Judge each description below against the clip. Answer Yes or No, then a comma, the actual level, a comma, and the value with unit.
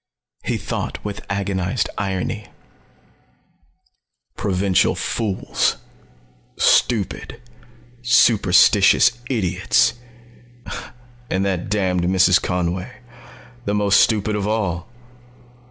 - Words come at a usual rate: No, slow, 75 wpm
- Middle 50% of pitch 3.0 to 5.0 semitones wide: No, narrow, 2.4 semitones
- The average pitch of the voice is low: Yes, low, 100 Hz